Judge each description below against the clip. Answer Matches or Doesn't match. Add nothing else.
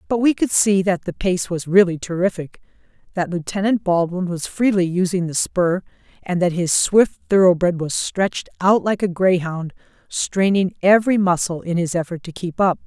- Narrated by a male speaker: Doesn't match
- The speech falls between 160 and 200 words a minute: Matches